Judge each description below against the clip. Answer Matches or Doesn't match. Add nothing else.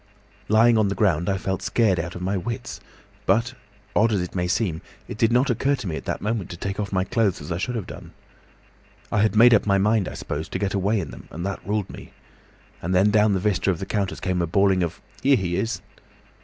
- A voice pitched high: Doesn't match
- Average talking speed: Doesn't match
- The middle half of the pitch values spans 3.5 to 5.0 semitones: Doesn't match